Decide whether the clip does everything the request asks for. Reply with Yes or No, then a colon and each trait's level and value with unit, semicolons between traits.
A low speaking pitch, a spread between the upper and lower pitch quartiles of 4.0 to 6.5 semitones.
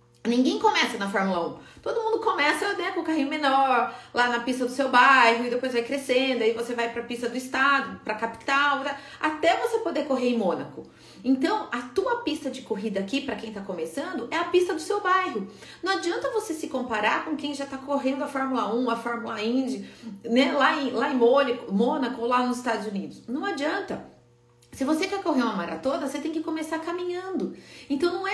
No: very high, 270 Hz; average, 5.3 semitones